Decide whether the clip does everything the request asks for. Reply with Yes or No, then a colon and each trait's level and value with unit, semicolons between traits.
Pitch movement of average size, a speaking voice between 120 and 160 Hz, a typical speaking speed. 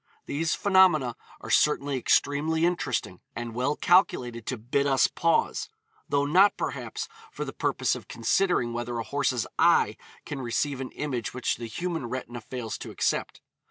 Yes: average, 4.8 semitones; low, 135 Hz; average, 160 wpm